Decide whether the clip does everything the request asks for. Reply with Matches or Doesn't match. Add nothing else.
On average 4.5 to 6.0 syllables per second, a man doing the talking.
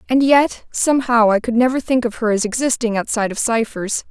Doesn't match